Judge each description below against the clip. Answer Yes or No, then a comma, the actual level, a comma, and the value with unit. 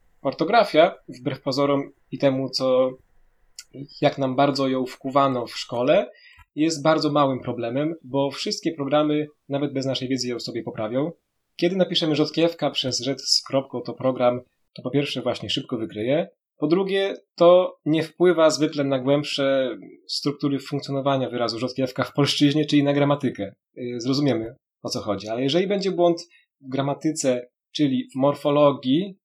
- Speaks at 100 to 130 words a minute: No, average, 150 wpm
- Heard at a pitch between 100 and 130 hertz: No, medium, 140 Hz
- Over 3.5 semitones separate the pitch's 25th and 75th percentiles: No, average, 2.8 semitones